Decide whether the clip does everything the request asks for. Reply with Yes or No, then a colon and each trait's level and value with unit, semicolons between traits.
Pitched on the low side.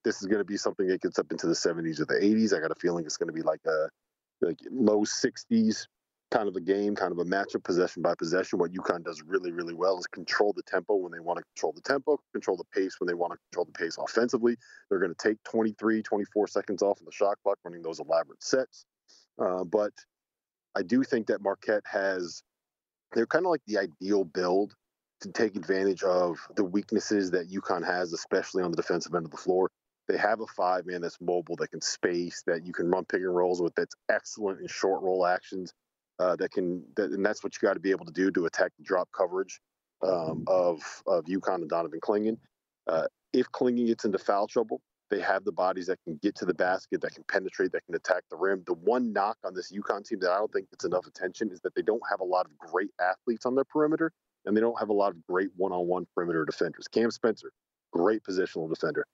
Yes: low, 105 Hz